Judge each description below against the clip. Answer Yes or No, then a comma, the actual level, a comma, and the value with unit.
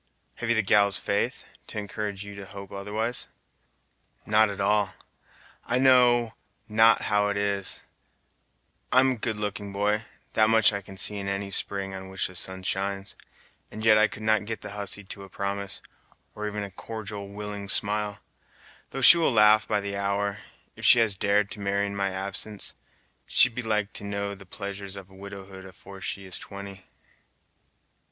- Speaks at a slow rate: No, average, 175 wpm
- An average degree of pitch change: No, narrow, 1.4 semitones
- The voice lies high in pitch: No, low, 100 Hz